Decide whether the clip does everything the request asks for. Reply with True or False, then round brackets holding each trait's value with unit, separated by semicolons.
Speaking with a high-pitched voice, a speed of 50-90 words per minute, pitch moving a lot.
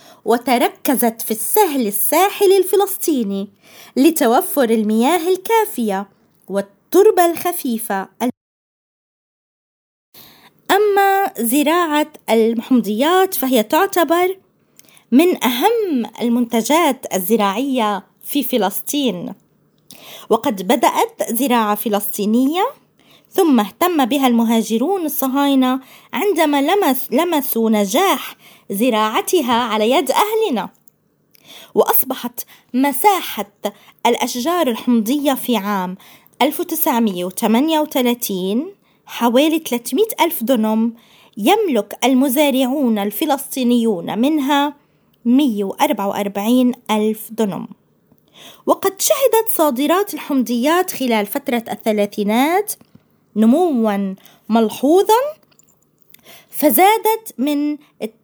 True (260 Hz; 70 wpm; 6.3 semitones)